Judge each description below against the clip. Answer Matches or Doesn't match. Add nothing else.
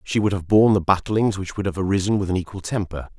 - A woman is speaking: Doesn't match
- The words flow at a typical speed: Doesn't match